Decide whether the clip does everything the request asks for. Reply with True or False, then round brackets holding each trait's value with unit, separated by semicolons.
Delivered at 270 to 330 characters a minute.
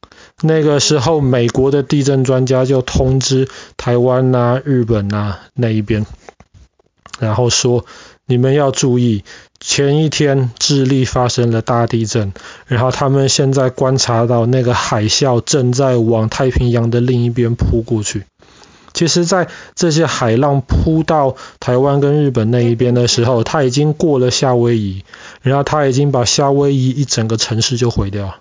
False (240 characters per minute)